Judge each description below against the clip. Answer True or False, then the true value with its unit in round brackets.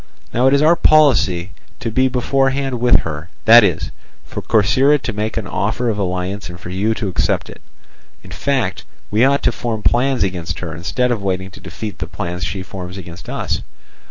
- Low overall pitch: True (105 Hz)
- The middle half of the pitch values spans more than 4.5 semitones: True (5.3 semitones)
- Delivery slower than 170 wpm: False (190 wpm)